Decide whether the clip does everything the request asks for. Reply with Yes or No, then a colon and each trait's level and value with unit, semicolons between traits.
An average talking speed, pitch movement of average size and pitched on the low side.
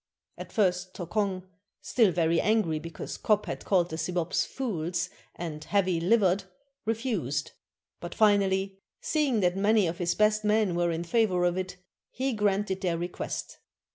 No: average, 150 wpm; average, 3.5 semitones; medium, 185 Hz